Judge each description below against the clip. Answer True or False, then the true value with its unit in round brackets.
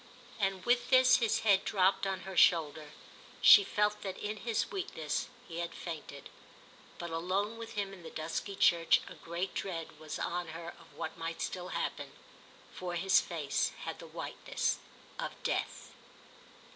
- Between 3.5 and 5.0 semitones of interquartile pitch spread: True (3.8 semitones)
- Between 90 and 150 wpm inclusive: False (160 wpm)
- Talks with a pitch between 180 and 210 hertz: True (185 Hz)